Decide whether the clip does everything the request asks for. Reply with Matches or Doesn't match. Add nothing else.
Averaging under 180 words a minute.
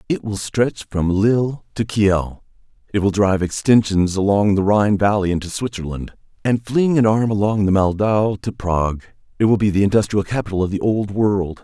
Doesn't match